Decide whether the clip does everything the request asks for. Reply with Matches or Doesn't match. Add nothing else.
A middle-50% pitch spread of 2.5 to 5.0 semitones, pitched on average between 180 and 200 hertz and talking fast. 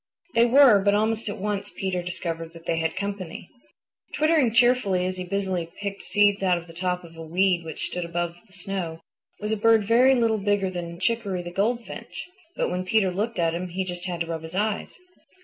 Matches